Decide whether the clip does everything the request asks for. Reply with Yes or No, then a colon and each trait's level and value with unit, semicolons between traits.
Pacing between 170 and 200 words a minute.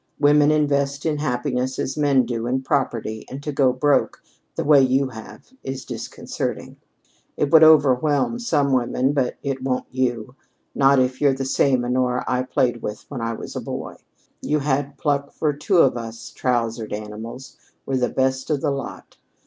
Yes: average, 175 wpm